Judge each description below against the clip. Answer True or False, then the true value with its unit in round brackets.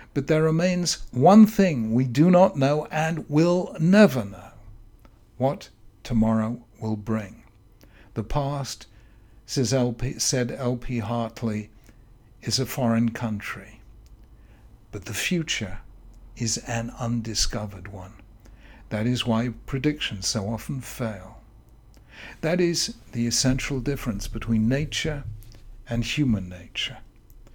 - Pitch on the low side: True (115 Hz)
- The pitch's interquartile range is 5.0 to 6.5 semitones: False (3.5 semitones)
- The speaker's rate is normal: False (115 wpm)